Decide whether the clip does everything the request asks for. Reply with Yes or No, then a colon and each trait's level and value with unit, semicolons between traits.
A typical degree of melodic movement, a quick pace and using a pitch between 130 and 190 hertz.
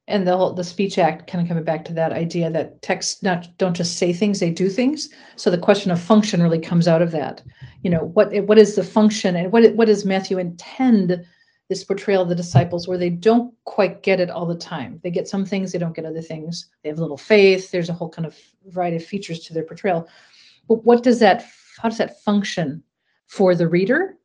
Yes: average, 3.5 semitones; fast, 235 wpm; medium, 185 Hz